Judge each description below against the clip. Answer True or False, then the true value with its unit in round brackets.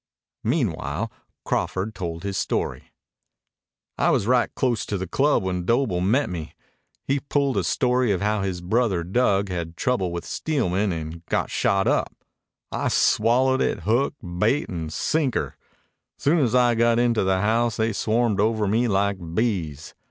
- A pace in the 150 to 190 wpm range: True (160 wpm)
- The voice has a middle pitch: False (110 Hz)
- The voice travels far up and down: False (4.7 semitones)